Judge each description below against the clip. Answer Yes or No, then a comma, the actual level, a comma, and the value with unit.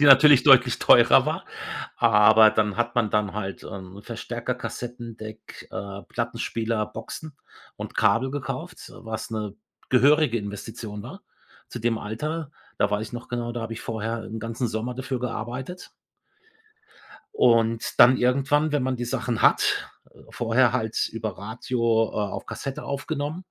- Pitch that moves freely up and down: No, narrow, 2.6 semitones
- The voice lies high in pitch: No, low, 115 Hz